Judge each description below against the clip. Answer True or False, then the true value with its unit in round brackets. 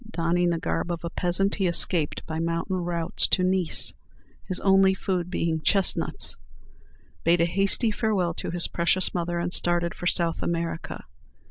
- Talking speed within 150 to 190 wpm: True (160 wpm)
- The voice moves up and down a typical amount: False (1.9 semitones)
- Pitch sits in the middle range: True (175 Hz)